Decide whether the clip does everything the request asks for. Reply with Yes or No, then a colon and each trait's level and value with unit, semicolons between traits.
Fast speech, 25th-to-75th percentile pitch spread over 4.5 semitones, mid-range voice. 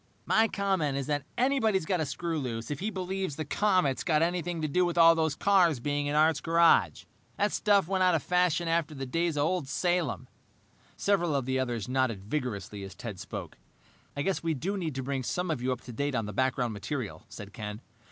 Yes: fast, 220 wpm; wide, 5.5 semitones; medium, 155 Hz